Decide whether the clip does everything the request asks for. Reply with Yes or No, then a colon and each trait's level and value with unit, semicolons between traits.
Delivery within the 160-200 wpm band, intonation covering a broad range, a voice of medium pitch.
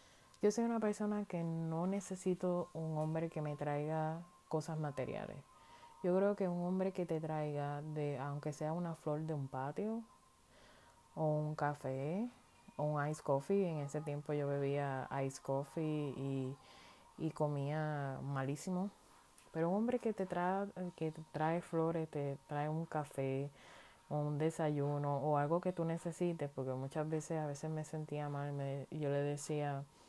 No: average, 165 wpm; average, 2.8 semitones; medium, 155 Hz